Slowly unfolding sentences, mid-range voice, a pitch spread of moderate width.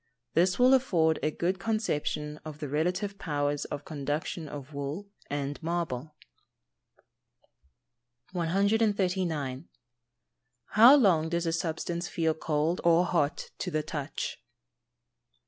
Yes: slow, 110 wpm; medium, 165 Hz; average, 3.6 semitones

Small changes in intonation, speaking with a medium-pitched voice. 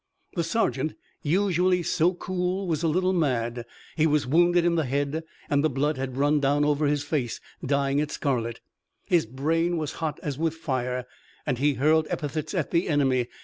No: average, 3.4 semitones; medium, 150 Hz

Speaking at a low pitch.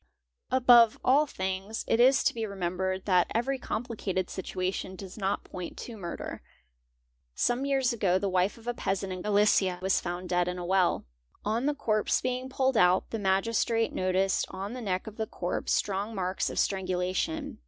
No: high, 200 Hz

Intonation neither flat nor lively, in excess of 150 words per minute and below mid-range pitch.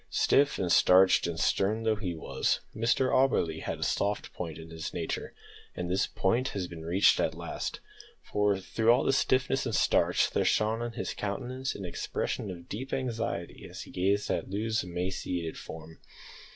Yes: average, 4.7 semitones; average, 180 wpm; low, 100 Hz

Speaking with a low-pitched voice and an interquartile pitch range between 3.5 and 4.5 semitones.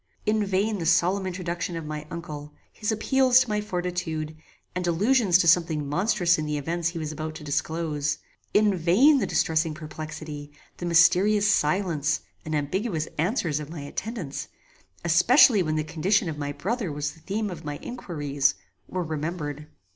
No: medium, 170 Hz; average, 4.2 semitones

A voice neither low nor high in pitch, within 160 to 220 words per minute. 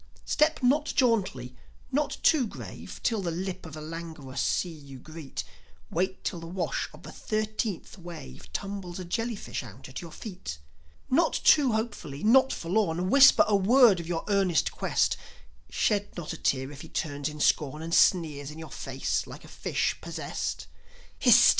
Yes: medium, 175 Hz; average, 170 wpm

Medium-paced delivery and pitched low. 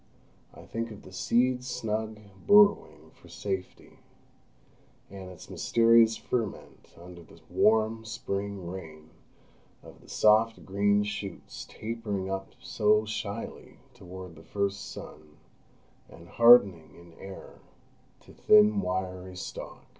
No: slow, 115 wpm; low, 100 Hz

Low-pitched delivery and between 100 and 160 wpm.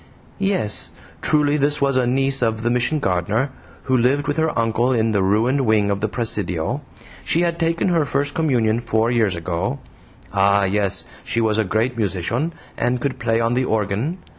No: low, 120 Hz; average, 185 wpm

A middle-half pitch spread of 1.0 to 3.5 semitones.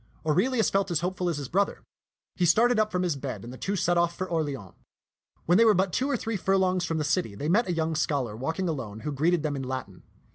No: average, 4.8 semitones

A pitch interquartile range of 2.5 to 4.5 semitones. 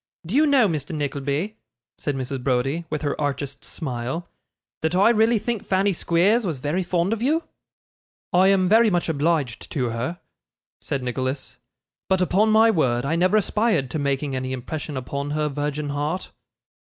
No: wide, 5.6 semitones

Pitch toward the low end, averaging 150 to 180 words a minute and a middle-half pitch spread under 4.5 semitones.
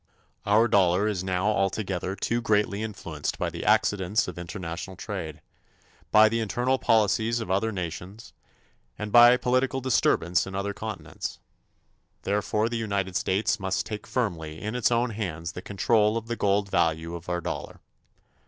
Yes: low, 100 Hz; average, 155 wpm; average, 3.2 semitones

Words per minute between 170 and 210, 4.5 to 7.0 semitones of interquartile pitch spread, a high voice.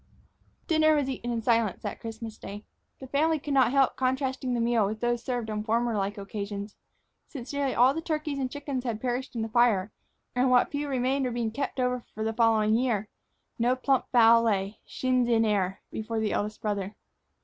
No: average, 200 wpm; average, 3.2 semitones; high, 240 Hz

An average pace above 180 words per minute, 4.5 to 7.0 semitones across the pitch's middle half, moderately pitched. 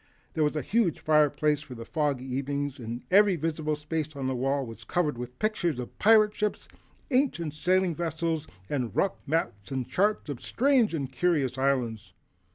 No: average, 165 wpm; average, 4.8 semitones; medium, 150 Hz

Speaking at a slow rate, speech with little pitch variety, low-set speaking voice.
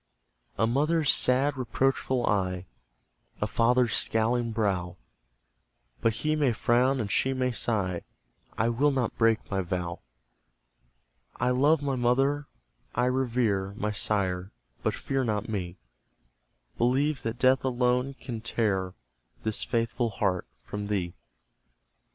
No: slow, 125 wpm; average, 3.9 semitones; low, 115 Hz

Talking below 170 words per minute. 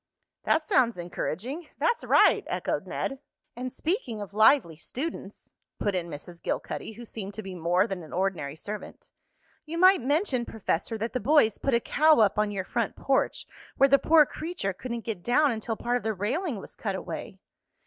No: average, 185 wpm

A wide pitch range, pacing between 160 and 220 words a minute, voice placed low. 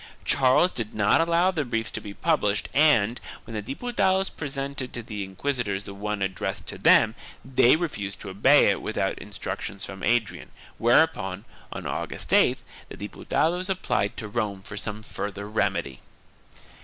Yes: wide, 6.0 semitones; average, 165 wpm; low, 115 Hz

